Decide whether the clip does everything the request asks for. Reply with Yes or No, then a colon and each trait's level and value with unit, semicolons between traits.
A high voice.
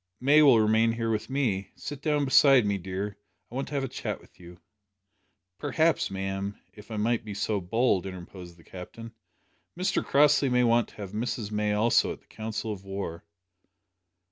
No: low, 110 Hz